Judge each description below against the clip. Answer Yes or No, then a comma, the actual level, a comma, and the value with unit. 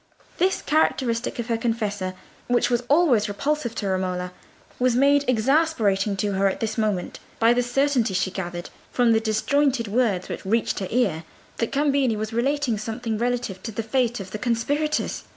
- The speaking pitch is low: No, high, 230 Hz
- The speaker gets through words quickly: No, average, 170 wpm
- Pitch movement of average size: Yes, average, 3.8 semitones